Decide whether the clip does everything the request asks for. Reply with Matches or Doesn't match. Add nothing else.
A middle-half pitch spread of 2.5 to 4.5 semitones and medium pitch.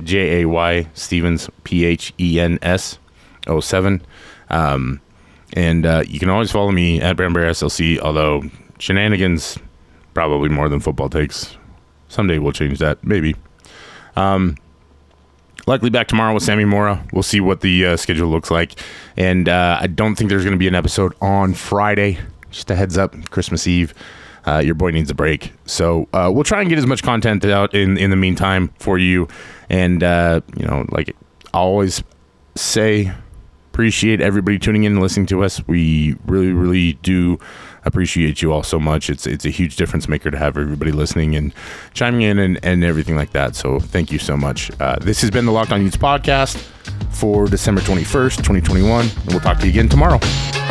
Doesn't match